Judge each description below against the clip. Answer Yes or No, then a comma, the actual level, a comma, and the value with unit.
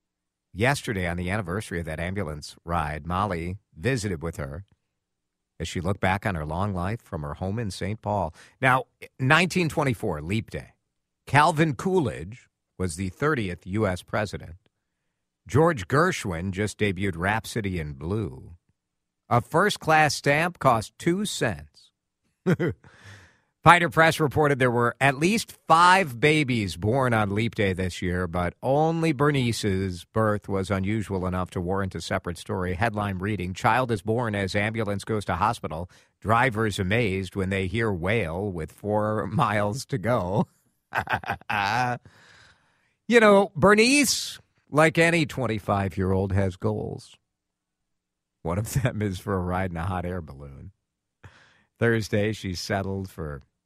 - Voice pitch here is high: No, low, 105 Hz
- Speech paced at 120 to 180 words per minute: Yes, average, 140 wpm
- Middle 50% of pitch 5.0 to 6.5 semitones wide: Yes, wide, 5.5 semitones